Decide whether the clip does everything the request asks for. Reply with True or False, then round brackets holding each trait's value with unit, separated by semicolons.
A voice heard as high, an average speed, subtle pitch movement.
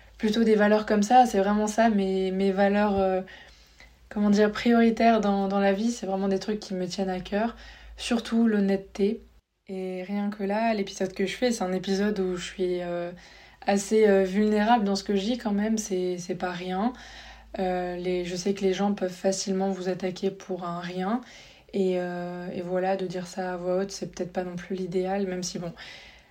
True (195 Hz; 210 wpm; 2.3 semitones)